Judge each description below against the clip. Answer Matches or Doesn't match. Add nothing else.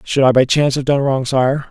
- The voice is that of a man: Matches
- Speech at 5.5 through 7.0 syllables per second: Matches